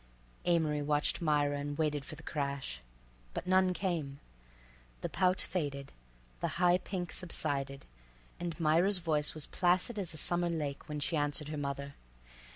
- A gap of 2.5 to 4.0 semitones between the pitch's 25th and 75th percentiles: Yes, average, 3.7 semitones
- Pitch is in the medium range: Yes, medium, 150 Hz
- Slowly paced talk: No, average, 150 wpm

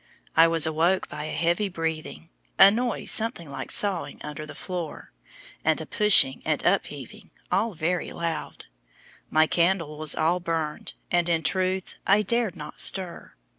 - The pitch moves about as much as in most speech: Yes, average, 3.2 semitones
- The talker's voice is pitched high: No, medium, 170 Hz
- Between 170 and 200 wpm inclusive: No, average, 155 wpm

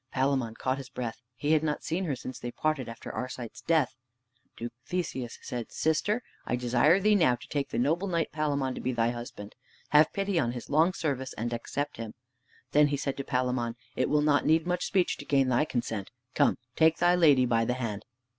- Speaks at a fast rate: Yes, fast, 210 wpm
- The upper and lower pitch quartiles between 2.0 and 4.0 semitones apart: No, average, 4.6 semitones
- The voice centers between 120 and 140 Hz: Yes, low, 135 Hz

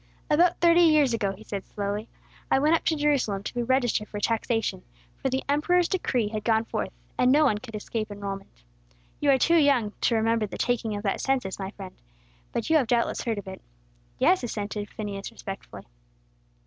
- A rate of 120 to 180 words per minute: No, average, 195 wpm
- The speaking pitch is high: Yes, high, 230 Hz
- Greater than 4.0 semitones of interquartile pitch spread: Yes, average, 5.2 semitones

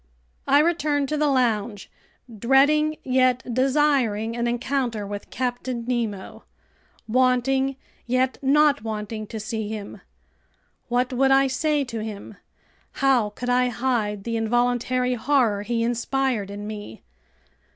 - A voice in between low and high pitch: No, high, 245 Hz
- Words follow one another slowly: Yes, slow, 125 wpm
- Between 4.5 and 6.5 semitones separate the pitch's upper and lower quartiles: No, average, 3.4 semitones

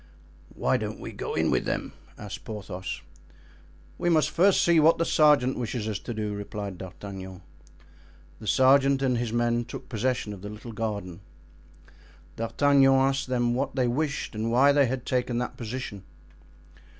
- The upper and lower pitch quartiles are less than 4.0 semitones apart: No, average, 4.3 semitones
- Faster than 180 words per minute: No, average, 160 wpm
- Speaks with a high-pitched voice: No, low, 120 Hz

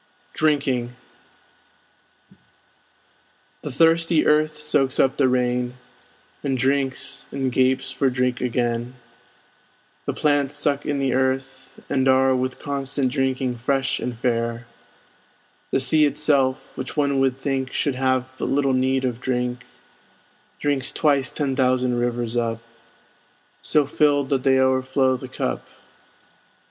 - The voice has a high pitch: No, low, 130 Hz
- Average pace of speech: No, slow, 125 wpm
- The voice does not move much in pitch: Yes, narrow, 1.7 semitones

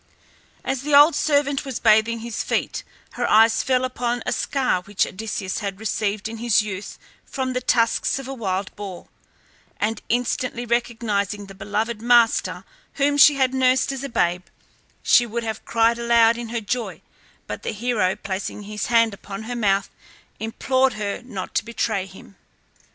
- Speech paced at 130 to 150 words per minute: No, average, 165 wpm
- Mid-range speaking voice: No, high, 230 Hz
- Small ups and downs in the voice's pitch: No, average, 3.3 semitones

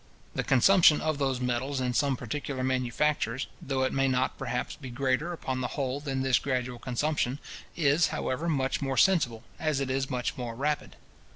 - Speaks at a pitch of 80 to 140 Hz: Yes, low, 135 Hz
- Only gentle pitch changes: Yes, narrow, 2.2 semitones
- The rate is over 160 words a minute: Yes, average, 180 wpm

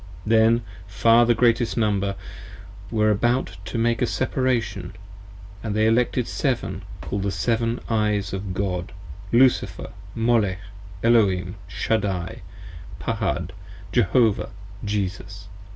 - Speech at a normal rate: No, slow, 110 wpm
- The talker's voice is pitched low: Yes, low, 110 Hz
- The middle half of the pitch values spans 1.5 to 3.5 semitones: Yes, average, 3.0 semitones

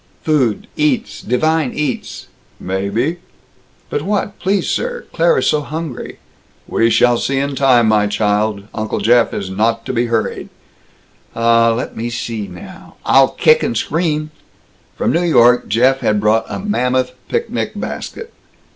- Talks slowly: No, average, 145 wpm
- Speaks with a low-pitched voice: Yes, low, 125 Hz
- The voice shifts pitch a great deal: Yes, wide, 6.2 semitones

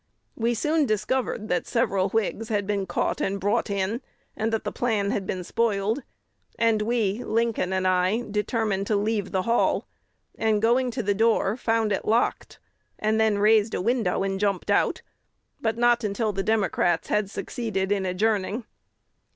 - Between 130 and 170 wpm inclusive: Yes, average, 165 wpm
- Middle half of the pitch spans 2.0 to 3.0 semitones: Yes, narrow, 2.5 semitones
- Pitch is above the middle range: Yes, high, 215 Hz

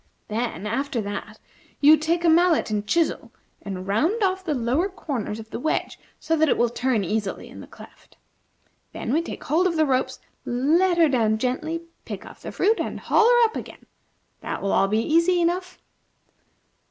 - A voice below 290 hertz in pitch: No, very high, 295 Hz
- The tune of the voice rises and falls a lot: Yes, wide, 7.3 semitones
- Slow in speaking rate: No, average, 190 wpm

